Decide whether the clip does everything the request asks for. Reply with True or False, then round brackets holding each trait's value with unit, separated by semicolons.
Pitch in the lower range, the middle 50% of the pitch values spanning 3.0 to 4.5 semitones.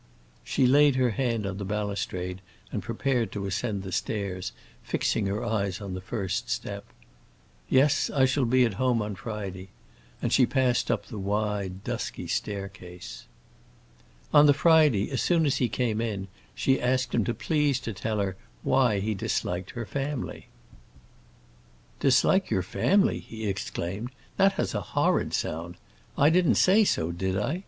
False (110 Hz; 5.3 semitones)